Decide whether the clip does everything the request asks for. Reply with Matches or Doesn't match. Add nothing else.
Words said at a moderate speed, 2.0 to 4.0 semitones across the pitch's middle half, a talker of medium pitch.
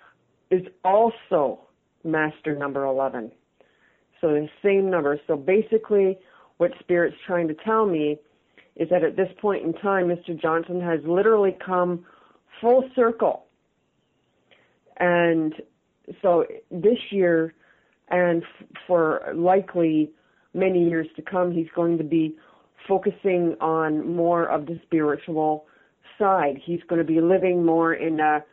Doesn't match